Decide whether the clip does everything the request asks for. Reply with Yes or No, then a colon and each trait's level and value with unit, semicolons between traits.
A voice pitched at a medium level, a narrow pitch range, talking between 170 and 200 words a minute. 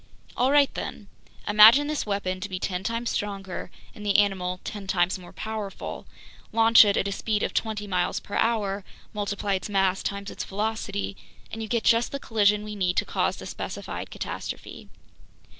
No: high, 205 Hz; narrow, 2.3 semitones; average, 180 wpm